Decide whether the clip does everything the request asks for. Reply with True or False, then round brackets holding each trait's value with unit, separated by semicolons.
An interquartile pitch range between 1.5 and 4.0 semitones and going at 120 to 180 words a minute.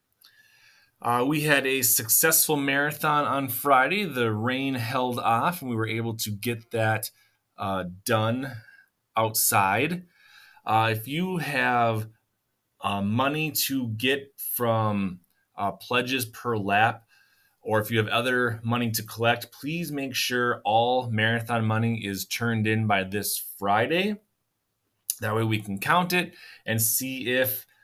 True (3.7 semitones; 140 wpm)